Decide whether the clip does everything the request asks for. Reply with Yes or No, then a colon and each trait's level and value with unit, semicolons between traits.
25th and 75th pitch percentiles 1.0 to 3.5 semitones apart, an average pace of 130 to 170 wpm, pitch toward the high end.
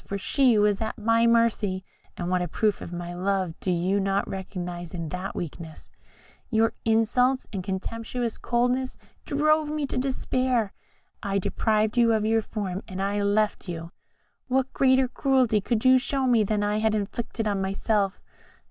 No: average, 4.0 semitones; average, 165 wpm; high, 215 Hz